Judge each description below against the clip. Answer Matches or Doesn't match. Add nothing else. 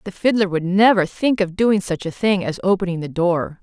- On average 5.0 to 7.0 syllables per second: Matches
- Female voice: Matches